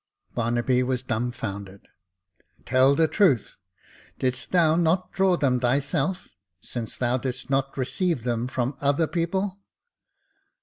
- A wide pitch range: No, average, 5.0 semitones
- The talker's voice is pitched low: Yes, low, 130 Hz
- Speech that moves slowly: Yes, slow, 120 wpm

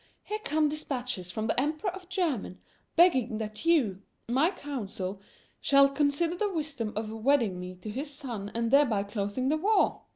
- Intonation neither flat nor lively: No, wide, 6.3 semitones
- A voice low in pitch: No, very high, 265 Hz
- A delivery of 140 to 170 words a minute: Yes, average, 165 wpm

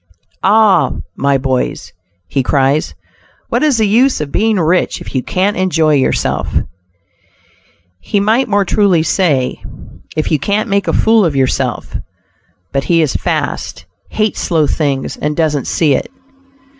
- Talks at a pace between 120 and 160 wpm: Yes, average, 145 wpm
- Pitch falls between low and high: Yes, medium, 165 Hz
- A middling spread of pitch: No, wide, 6.3 semitones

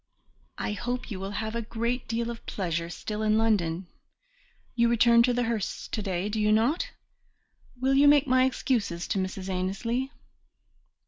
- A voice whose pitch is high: Yes, high, 225 Hz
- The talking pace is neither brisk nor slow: Yes, average, 160 wpm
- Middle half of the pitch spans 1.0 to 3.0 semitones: No, average, 3.8 semitones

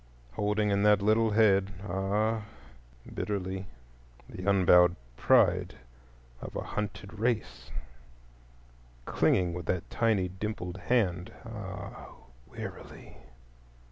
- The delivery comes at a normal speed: No, slow, 80 wpm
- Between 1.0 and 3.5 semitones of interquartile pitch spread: Yes, average, 2.8 semitones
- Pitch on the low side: Yes, low, 100 Hz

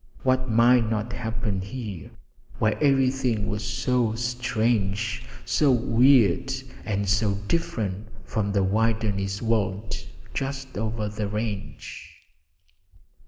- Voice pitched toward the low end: Yes, low, 110 Hz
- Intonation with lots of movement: No, average, 3.1 semitones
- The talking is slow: Yes, slow, 105 wpm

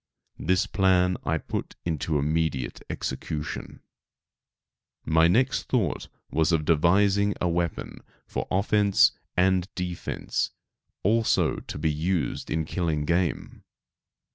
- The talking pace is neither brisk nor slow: No, slow, 110 wpm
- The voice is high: No, very low, 85 Hz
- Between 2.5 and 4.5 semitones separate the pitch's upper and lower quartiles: Yes, average, 3.0 semitones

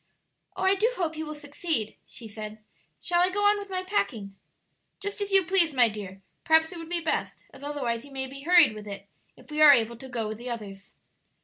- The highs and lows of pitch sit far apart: Yes, wide, 7.8 semitones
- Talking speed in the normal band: No, fast, 230 wpm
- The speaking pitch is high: Yes, very high, 290 Hz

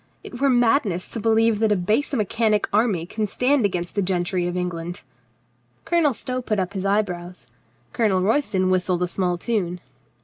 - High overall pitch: Yes, high, 200 Hz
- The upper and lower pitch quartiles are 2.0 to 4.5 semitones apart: Yes, average, 4.1 semitones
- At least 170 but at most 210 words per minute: Yes, average, 175 wpm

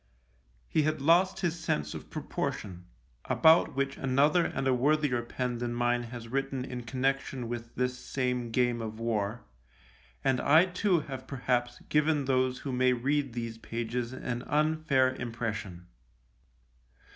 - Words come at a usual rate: Yes, average, 155 wpm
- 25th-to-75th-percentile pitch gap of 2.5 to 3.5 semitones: Yes, average, 2.9 semitones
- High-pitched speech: No, low, 125 Hz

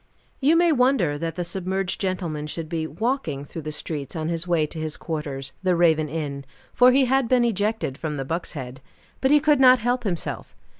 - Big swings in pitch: Yes, wide, 7.9 semitones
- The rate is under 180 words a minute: No, fast, 205 wpm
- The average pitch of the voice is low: No, medium, 170 Hz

